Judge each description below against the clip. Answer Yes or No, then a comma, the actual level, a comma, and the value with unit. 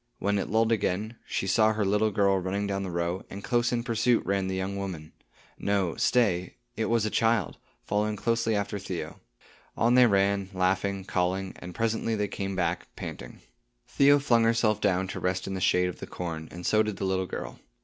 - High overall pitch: No, low, 100 Hz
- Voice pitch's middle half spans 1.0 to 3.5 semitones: Yes, average, 2.9 semitones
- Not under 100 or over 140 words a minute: No, average, 200 wpm